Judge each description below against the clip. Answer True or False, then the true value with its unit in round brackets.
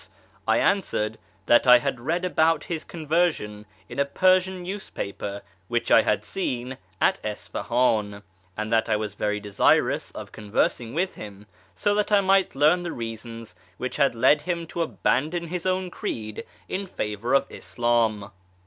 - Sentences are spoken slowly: False (155 wpm)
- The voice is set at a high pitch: False (125 Hz)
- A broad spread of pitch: True (8.3 semitones)